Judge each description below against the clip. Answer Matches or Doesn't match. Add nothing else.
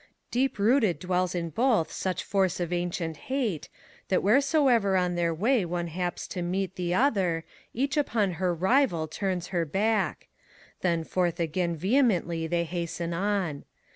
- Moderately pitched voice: Matches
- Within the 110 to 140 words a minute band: Doesn't match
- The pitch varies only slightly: Doesn't match